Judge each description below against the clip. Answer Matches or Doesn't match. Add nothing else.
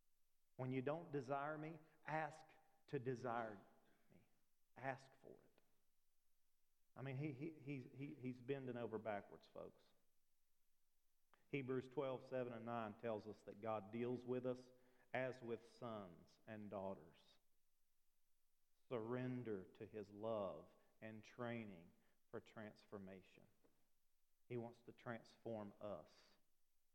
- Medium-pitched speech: Doesn't match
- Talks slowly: Matches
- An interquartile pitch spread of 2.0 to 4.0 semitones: Matches